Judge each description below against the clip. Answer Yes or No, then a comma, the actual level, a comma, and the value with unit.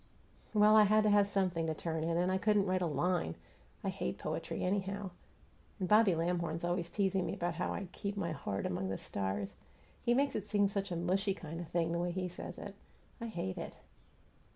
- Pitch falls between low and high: Yes, medium, 180 Hz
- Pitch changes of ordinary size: Yes, average, 3.2 semitones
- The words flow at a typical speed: No, fast, 215 wpm